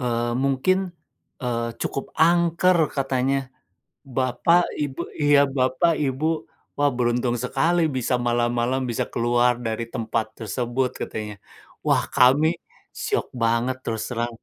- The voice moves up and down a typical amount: Yes, average, 3.3 semitones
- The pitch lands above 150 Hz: No, low, 130 Hz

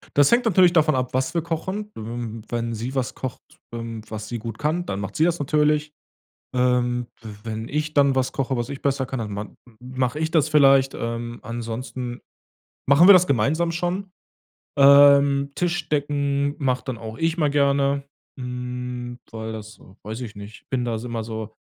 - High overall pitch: No, low, 130 Hz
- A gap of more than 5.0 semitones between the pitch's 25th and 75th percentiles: No, average, 4.2 semitones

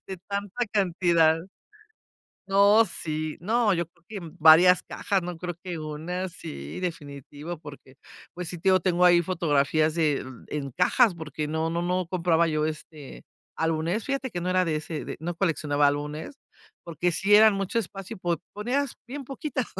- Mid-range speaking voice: Yes, medium, 175 Hz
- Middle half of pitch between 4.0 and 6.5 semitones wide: No, average, 3.6 semitones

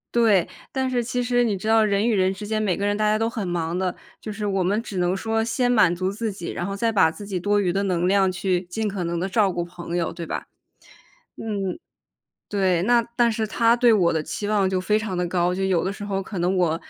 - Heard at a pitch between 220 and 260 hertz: No, high, 200 Hz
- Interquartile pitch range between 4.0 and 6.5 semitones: No, average, 3.4 semitones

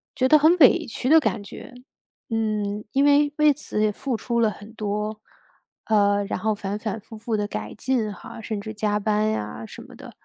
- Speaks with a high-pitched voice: Yes, high, 215 Hz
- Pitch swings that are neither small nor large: Yes, average, 3.1 semitones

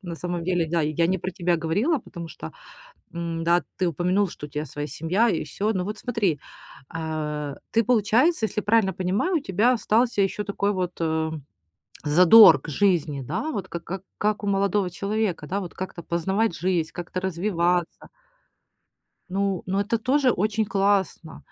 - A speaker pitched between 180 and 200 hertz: Yes, medium, 185 Hz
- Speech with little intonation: No, average, 3.8 semitones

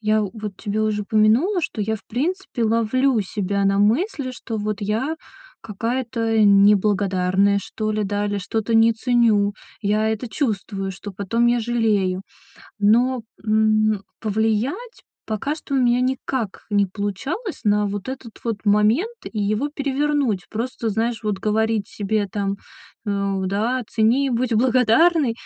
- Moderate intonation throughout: Yes, average, 3.0 semitones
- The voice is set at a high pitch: Yes, high, 220 Hz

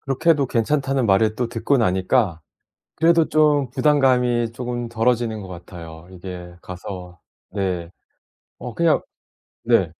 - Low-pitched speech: Yes, low, 115 Hz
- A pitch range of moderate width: No, wide, 6.4 semitones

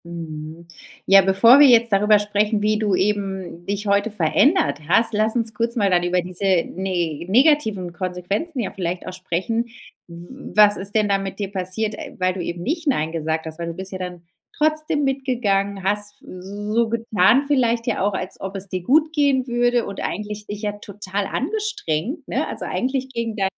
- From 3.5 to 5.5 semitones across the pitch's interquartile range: Yes, average, 4.1 semitones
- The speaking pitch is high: Yes, high, 205 Hz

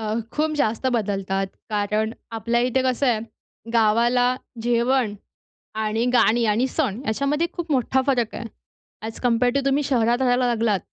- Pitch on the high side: Yes, high, 235 Hz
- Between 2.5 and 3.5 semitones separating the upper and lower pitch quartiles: Yes, average, 2.9 semitones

